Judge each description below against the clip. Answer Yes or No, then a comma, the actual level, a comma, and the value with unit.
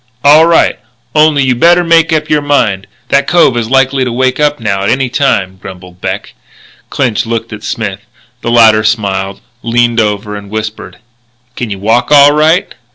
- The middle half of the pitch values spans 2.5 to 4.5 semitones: No, wide, 5.5 semitones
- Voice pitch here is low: Yes, low, 120 Hz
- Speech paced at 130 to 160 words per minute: No, average, 175 wpm